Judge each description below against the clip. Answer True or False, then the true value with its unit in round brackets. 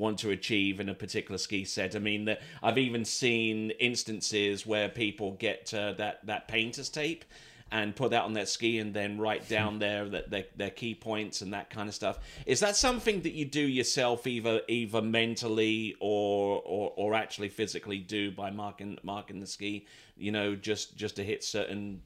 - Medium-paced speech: True (195 wpm)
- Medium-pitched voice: False (105 Hz)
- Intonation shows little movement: True (2.2 semitones)